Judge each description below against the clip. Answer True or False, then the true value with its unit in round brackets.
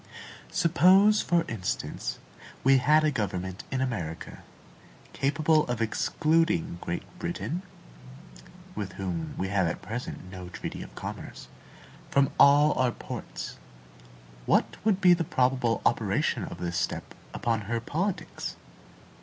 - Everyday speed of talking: False (125 wpm)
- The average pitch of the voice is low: True (130 Hz)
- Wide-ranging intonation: True (8.6 semitones)